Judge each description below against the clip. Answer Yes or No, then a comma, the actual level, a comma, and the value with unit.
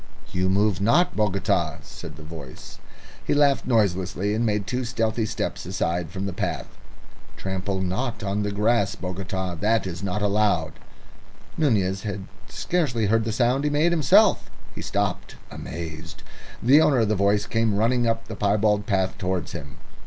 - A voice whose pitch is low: Yes, low, 105 Hz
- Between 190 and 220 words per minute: No, average, 160 wpm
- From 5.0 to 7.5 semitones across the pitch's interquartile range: No, average, 3.4 semitones